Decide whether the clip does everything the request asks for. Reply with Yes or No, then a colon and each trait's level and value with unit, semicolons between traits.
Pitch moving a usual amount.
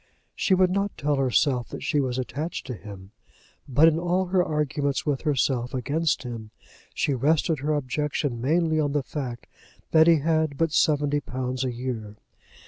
Yes: average, 3.8 semitones